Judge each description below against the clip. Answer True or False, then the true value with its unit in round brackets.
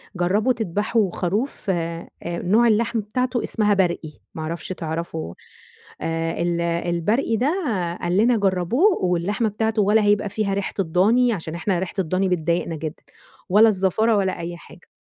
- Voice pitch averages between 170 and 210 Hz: True (190 Hz)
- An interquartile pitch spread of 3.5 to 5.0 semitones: True (4.2 semitones)